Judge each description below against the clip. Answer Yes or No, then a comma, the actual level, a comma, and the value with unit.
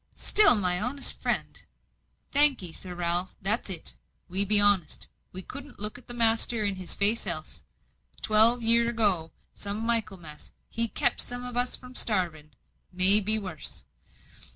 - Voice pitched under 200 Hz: No, high, 210 Hz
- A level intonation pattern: No, average, 4.4 semitones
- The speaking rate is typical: Yes, average, 155 wpm